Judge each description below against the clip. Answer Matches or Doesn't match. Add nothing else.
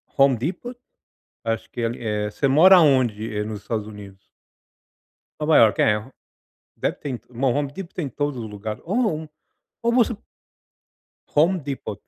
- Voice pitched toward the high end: Doesn't match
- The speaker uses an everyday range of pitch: Doesn't match